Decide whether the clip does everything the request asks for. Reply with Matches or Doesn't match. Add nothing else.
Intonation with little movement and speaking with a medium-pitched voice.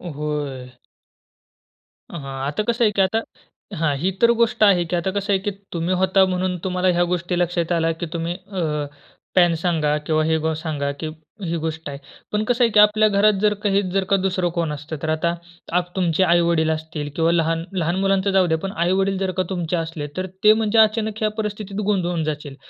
Doesn't match